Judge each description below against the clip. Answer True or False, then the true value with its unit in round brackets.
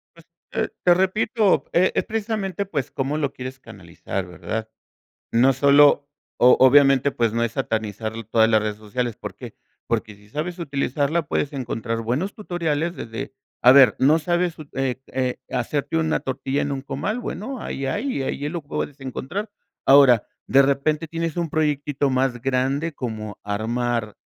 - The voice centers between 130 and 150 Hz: True (135 Hz)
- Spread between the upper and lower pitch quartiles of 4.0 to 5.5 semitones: True (5.0 semitones)